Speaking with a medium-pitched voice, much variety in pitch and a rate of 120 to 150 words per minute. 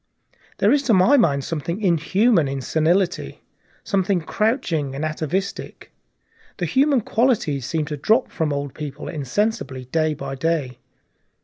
Yes: medium, 165 Hz; wide, 6.5 semitones; slow, 135 wpm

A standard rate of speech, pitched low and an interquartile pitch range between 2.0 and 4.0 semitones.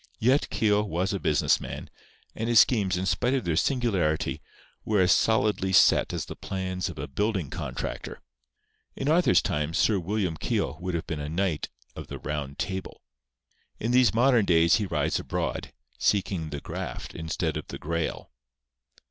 No: average, 170 wpm; very low, 95 Hz; average, 4.8 semitones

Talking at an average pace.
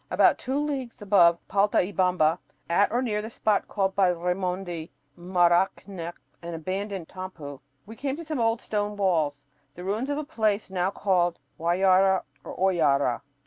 Yes: average, 150 wpm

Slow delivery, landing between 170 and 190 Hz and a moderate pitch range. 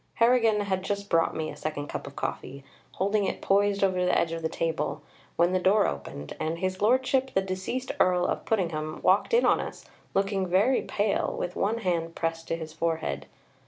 No: average, 195 wpm; medium, 185 Hz; average, 3.7 semitones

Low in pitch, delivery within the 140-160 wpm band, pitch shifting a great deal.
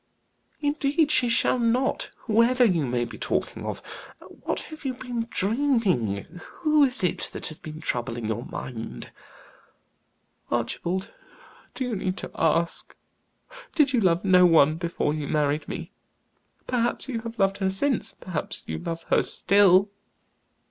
No: high, 190 Hz; average, 145 wpm; wide, 8.1 semitones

